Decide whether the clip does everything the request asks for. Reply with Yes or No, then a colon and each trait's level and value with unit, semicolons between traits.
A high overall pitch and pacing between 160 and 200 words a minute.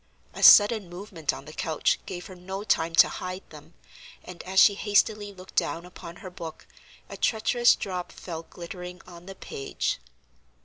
No: medium, 180 Hz; average, 170 wpm